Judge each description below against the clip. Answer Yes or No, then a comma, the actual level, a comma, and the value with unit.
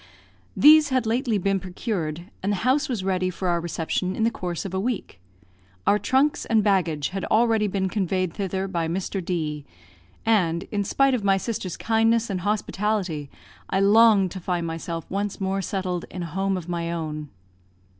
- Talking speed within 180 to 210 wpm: Yes, average, 185 wpm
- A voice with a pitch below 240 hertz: Yes, high, 190 Hz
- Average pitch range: Yes, average, 3.8 semitones